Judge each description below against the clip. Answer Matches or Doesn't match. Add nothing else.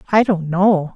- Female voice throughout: Matches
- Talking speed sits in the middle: Matches